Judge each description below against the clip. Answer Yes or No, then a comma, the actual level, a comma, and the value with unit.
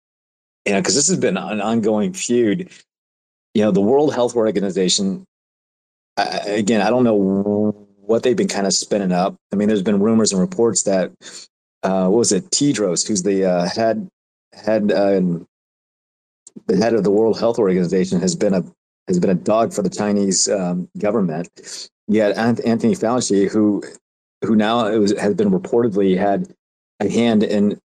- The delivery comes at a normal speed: Yes, average, 170 wpm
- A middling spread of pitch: Yes, average, 3.4 semitones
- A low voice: Yes, low, 105 Hz